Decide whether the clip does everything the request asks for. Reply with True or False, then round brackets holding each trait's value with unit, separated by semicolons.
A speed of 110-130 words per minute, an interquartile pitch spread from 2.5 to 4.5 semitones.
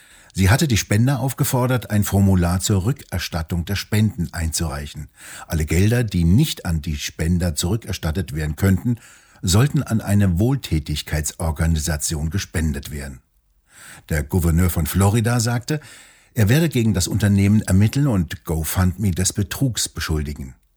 False (125 wpm; 5.3 semitones)